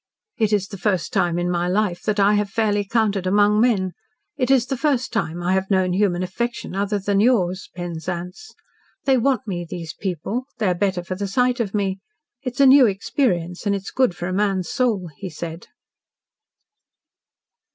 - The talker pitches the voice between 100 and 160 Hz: No, high, 200 Hz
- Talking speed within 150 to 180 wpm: No, average, 190 wpm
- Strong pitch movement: No, average, 4.0 semitones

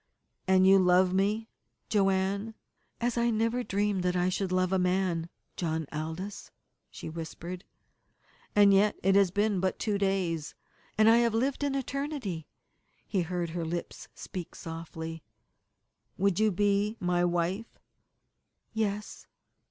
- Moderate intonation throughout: Yes, average, 3.0 semitones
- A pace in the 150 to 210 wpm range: No, average, 140 wpm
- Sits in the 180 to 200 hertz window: Yes, high, 190 Hz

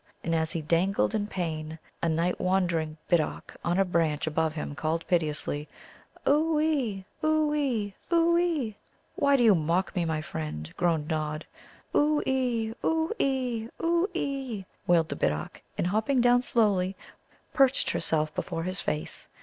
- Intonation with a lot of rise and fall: Yes, wide, 8.6 semitones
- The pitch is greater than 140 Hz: Yes, high, 190 Hz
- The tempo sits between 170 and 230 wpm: No, average, 155 wpm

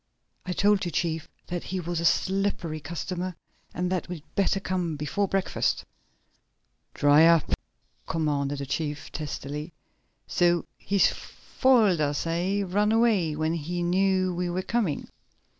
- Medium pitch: Yes, medium, 175 Hz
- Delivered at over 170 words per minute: No, average, 140 wpm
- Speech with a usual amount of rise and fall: Yes, average, 3.4 semitones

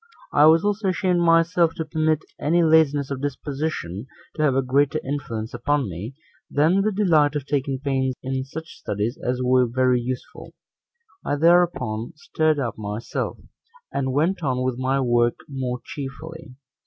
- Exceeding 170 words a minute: No, average, 155 wpm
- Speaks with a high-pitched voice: No, medium, 140 Hz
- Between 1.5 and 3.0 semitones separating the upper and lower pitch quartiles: No, average, 3.9 semitones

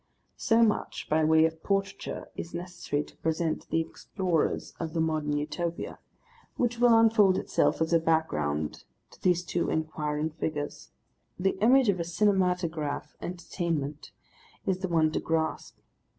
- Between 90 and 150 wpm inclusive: Yes, average, 145 wpm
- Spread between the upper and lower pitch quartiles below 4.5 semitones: Yes, average, 3.1 semitones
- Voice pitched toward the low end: No, medium, 165 Hz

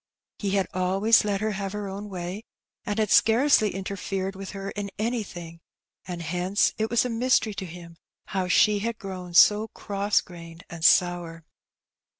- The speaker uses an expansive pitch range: No, average, 2.8 semitones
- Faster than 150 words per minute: Yes, average, 165 wpm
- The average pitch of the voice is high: Yes, high, 195 Hz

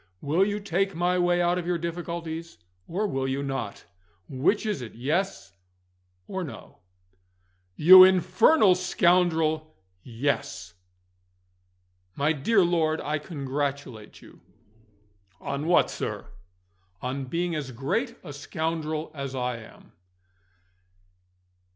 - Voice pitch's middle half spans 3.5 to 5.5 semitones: Yes, average, 4.4 semitones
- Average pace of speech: No, slow, 115 wpm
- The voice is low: No, medium, 160 Hz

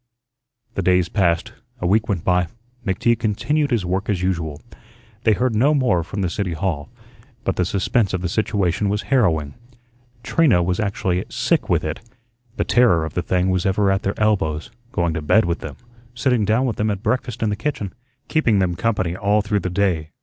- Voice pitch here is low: Yes, very low, 95 Hz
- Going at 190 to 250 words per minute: Yes, average, 195 wpm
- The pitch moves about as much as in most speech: Yes, average, 3.7 semitones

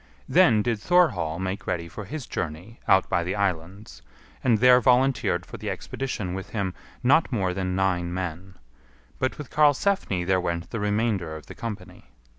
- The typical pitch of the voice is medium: No, very low, 95 Hz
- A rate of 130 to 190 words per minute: Yes, average, 170 wpm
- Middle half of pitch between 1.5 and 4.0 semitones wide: No, average, 5.0 semitones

